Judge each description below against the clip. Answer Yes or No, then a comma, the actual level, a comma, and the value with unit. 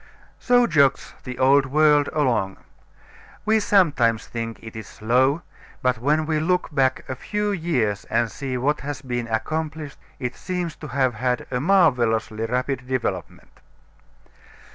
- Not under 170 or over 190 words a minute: No, average, 140 wpm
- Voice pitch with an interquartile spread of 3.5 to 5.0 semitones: Yes, average, 4.6 semitones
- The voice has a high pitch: No, low, 130 Hz